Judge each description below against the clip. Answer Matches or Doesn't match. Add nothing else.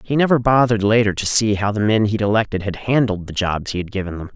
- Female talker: Doesn't match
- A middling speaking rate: Doesn't match